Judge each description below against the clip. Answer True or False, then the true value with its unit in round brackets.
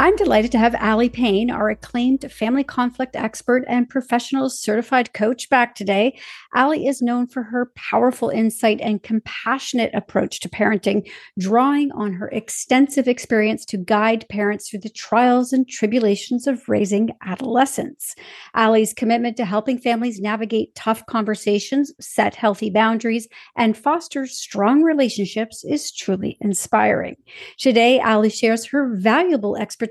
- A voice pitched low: False (235 Hz)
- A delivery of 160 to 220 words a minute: False (140 wpm)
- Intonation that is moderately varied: True (3.2 semitones)